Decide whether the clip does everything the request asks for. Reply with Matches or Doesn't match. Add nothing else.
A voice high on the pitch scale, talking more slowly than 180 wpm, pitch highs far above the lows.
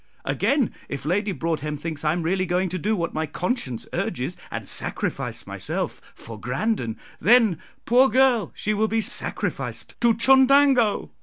Matches